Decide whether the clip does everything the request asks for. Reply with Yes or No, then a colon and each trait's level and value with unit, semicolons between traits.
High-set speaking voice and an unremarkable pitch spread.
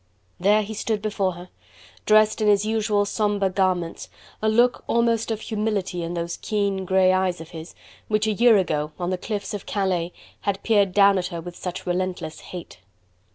Yes: high, 195 Hz; average, 3.0 semitones